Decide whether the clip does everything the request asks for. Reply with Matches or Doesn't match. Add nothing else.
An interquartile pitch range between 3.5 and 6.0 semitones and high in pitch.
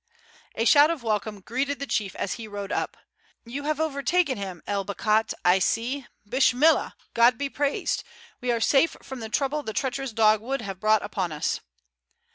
Matches